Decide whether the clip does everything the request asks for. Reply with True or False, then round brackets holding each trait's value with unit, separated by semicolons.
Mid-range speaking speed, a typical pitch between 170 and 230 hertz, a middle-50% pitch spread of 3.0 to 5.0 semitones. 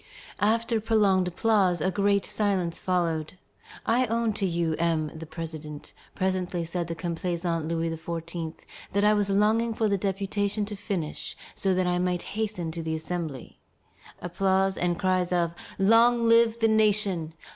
True (155 wpm; 185 Hz; 3.7 semitones)